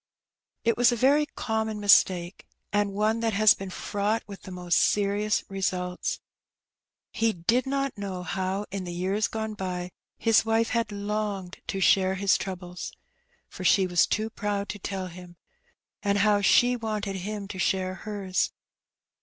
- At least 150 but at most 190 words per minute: Yes, average, 160 wpm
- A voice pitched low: No, high, 200 Hz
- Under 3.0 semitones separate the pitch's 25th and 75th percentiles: Yes, narrow, 2.6 semitones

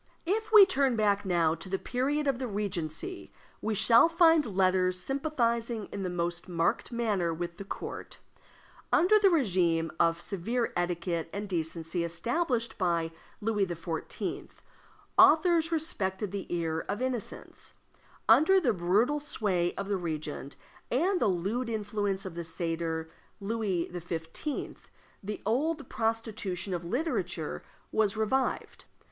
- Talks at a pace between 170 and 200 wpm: No, slow, 135 wpm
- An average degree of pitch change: No, wide, 6.4 semitones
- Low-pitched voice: No, high, 200 Hz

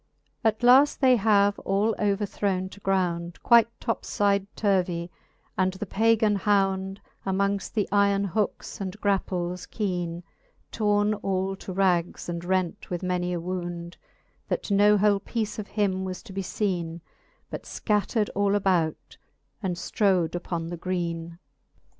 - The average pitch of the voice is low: No, high, 195 Hz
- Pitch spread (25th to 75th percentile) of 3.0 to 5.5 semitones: No, narrow, 2.5 semitones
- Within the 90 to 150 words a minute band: Yes, average, 140 wpm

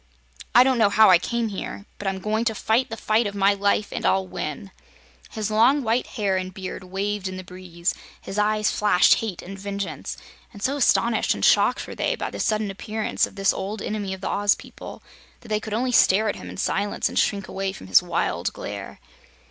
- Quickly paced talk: Yes, fast, 220 wpm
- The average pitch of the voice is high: Yes, high, 205 Hz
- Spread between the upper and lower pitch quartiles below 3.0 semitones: Yes, narrow, 2.4 semitones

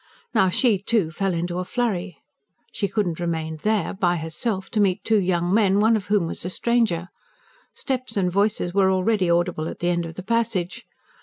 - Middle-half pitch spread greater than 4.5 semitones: No, average, 3.5 semitones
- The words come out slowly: No, average, 200 wpm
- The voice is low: No, high, 190 Hz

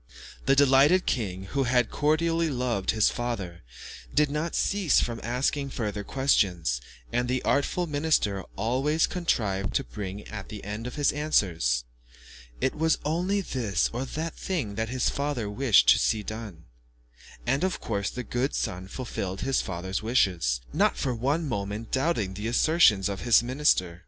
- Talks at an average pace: Yes, average, 160 wpm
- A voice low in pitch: Yes, low, 120 Hz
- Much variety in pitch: Yes, wide, 6.2 semitones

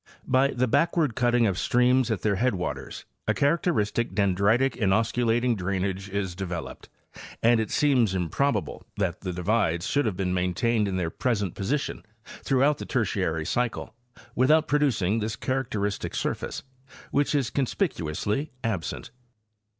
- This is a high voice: No, low, 110 Hz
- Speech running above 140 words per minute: No, slow, 135 wpm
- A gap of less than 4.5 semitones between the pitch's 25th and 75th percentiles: No, average, 5.2 semitones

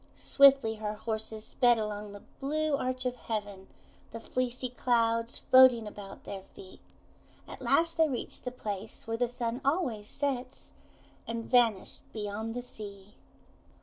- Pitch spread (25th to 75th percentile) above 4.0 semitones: No, average, 3.2 semitones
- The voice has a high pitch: Yes, high, 230 Hz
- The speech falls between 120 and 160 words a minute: Yes, average, 145 wpm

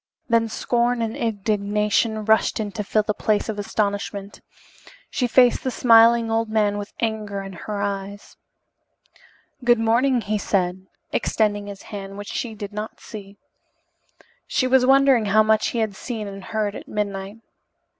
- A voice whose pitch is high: Yes, high, 215 Hz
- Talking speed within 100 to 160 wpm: Yes, average, 155 wpm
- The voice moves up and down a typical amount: No, narrow, 2.0 semitones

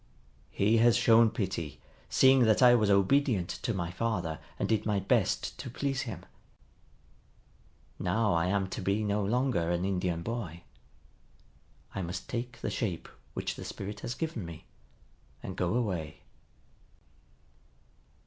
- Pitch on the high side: No, low, 100 Hz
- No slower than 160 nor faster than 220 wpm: No, average, 140 wpm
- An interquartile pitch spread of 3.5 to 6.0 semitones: Yes, average, 4.6 semitones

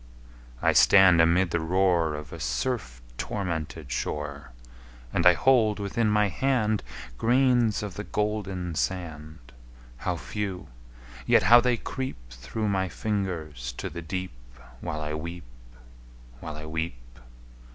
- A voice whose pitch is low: Yes, very low, 90 Hz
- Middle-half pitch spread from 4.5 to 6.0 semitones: Yes, wide, 5.5 semitones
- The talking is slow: Yes, slow, 130 wpm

